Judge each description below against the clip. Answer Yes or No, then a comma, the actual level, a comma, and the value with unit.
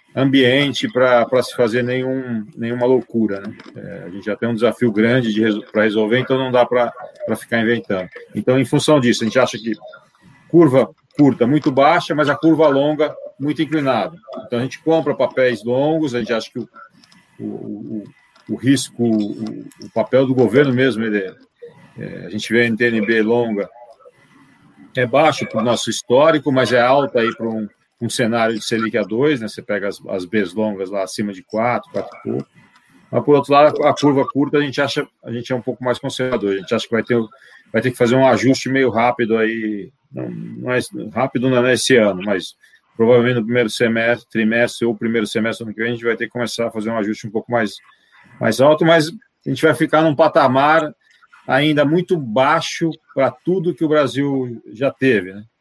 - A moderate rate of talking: No, fast, 205 wpm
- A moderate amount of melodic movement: Yes, average, 3.9 semitones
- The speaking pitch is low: Yes, low, 125 Hz